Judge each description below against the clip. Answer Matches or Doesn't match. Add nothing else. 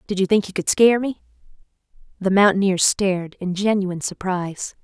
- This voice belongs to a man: Doesn't match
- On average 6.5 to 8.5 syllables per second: Doesn't match